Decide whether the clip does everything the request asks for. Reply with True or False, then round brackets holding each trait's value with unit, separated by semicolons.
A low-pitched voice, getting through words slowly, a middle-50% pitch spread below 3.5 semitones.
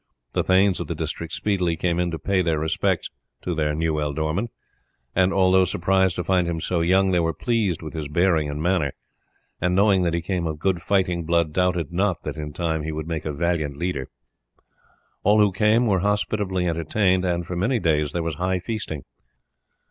False (85 Hz; 200 wpm; 2.9 semitones)